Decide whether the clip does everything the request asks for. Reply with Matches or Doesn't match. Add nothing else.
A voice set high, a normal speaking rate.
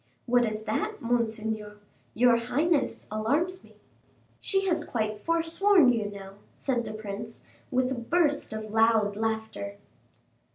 Doesn't match